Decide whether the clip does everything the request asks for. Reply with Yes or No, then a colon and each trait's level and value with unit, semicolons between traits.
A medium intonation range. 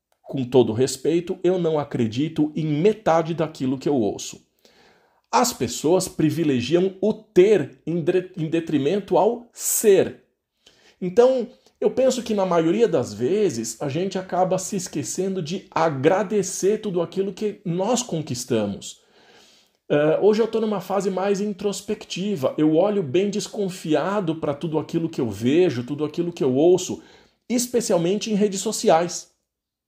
Yes: average, 4.9 semitones